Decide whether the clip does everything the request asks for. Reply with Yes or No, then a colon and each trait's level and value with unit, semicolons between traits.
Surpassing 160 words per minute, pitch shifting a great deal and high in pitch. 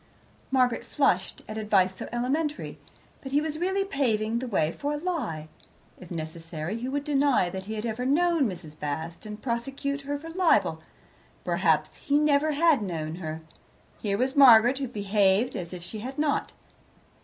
Yes: average, 170 wpm; wide, 7.2 semitones; high, 240 Hz